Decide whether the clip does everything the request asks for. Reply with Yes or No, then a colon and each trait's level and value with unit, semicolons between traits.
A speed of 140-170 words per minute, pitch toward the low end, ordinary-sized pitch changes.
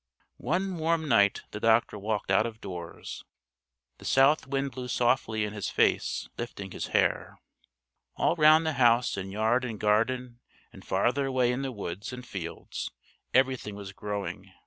Yes: average, 160 wpm; low, 120 Hz; average, 4.4 semitones